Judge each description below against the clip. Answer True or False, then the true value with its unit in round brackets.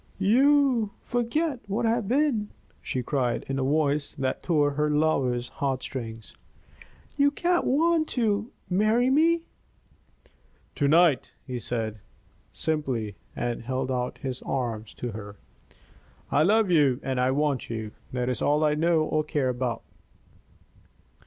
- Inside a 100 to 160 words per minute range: True (140 wpm)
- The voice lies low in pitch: False (150 Hz)